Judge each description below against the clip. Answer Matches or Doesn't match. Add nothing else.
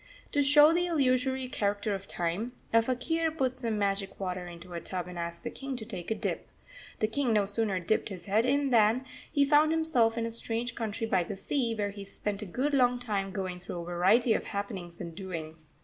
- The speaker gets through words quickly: Matches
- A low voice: Doesn't match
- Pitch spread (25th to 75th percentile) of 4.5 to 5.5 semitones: Matches